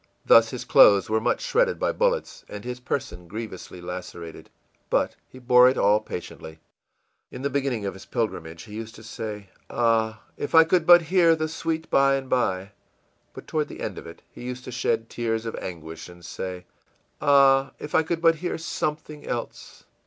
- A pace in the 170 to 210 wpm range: Yes, average, 190 wpm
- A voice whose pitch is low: Yes, low, 120 Hz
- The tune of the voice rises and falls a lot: Yes, wide, 6.7 semitones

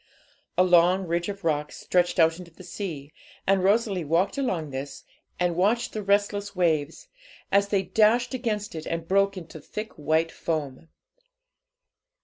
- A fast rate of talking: No, average, 150 wpm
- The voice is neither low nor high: Yes, medium, 180 Hz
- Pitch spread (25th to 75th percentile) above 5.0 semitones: No, average, 3.7 semitones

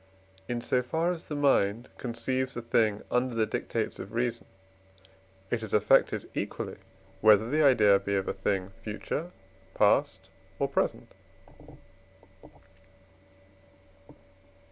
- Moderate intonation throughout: Yes, average, 3.8 semitones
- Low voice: Yes, low, 115 Hz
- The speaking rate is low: Yes, slow, 120 wpm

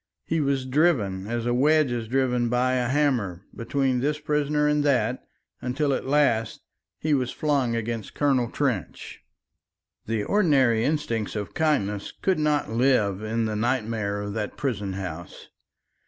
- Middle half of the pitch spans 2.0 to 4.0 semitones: No, average, 4.8 semitones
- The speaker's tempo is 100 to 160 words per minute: Yes, average, 150 wpm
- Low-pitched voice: Yes, low, 125 Hz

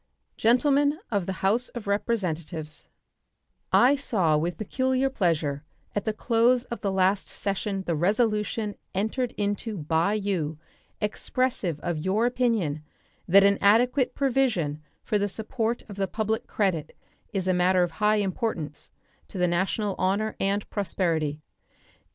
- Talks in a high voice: Yes, high, 200 Hz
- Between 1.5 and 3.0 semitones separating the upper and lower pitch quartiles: No, average, 4.3 semitones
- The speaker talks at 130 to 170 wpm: Yes, average, 140 wpm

